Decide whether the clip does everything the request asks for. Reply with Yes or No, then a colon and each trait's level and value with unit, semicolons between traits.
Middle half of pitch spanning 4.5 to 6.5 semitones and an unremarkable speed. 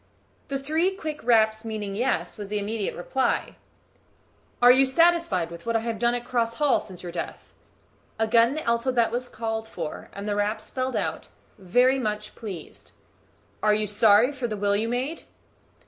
No: average, 3.5 semitones; average, 175 wpm